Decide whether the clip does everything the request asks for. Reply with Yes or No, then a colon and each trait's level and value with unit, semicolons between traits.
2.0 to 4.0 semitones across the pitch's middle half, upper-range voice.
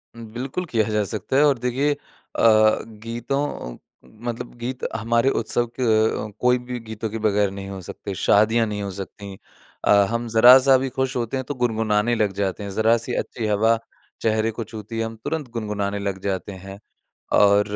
No: average, 2.8 semitones; low, 110 Hz